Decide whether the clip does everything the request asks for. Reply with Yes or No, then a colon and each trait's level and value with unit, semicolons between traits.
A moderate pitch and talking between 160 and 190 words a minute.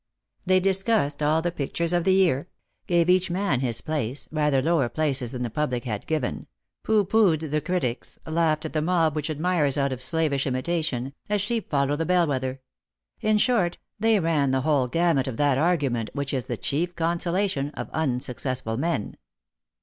Yes: medium, 155 Hz; average, 180 wpm